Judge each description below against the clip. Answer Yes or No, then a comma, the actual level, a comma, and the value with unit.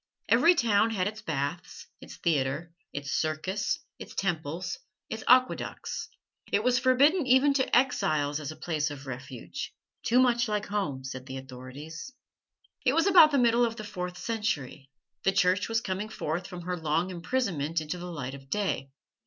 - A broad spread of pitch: Yes, wide, 7.5 semitones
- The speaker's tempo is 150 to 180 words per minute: Yes, average, 170 wpm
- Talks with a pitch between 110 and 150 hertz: No, medium, 180 Hz